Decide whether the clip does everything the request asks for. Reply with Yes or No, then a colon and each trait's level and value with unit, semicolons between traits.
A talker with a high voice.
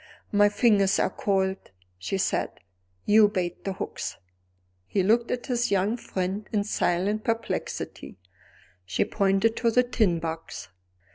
Yes: high, 200 Hz